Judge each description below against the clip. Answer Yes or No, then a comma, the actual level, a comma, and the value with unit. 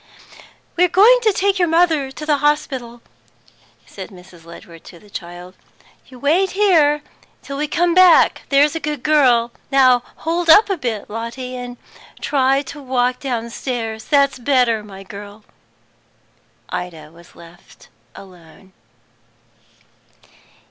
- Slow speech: Yes, slow, 125 wpm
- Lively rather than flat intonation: Yes, wide, 6.2 semitones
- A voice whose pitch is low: No, very high, 260 Hz